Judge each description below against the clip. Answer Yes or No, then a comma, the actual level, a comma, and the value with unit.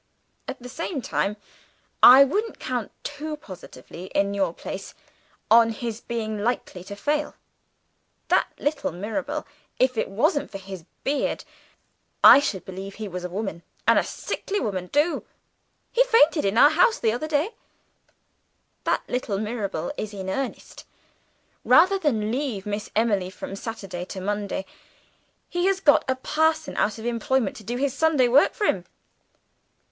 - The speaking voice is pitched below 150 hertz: No, high, 230 Hz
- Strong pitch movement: Yes, wide, 6.5 semitones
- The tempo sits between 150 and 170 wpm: Yes, average, 155 wpm